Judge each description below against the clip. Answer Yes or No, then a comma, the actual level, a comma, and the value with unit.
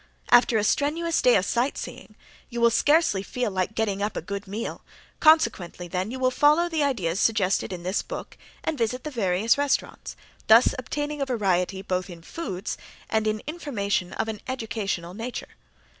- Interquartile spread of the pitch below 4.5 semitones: No, wide, 5.4 semitones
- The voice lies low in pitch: No, high, 220 Hz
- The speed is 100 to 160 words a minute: No, average, 175 wpm